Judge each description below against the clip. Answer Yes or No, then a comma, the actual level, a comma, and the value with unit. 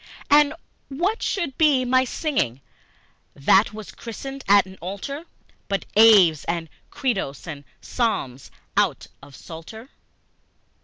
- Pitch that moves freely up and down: Yes, wide, 8.2 semitones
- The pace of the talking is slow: Yes, slow, 115 wpm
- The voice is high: Yes, high, 220 Hz